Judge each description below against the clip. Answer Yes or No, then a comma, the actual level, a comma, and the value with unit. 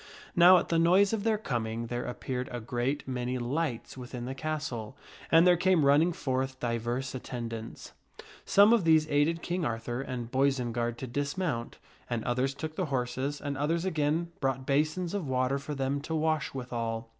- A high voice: No, low, 135 Hz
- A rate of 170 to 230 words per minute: Yes, average, 180 wpm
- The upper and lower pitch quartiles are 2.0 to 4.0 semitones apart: No, average, 4.6 semitones